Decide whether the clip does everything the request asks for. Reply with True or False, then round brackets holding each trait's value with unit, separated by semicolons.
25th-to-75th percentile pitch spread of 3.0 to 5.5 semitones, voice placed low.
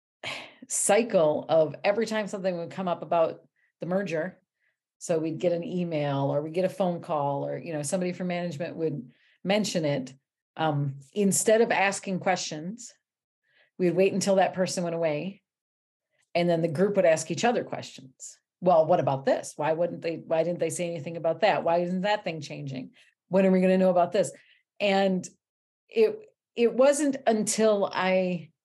False (3.4 semitones; 180 Hz)